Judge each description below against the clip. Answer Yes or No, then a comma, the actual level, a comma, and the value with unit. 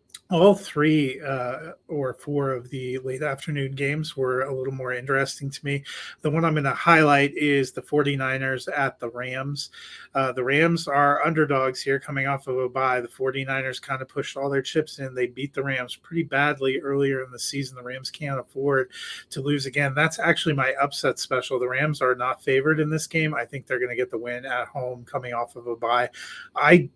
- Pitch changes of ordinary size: No, narrow, 2.2 semitones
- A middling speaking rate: No, fast, 210 wpm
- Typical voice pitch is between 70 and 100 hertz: No, low, 135 Hz